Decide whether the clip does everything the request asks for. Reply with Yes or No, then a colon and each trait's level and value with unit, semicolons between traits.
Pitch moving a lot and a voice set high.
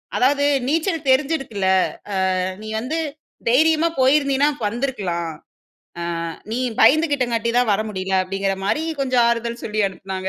Yes: wide, 6.1 semitones; high, 245 Hz